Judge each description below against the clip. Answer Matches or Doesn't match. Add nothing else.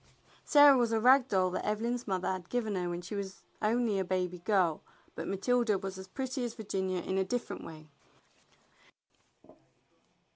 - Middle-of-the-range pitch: Doesn't match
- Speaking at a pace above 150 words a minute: Matches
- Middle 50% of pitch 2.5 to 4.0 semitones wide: Doesn't match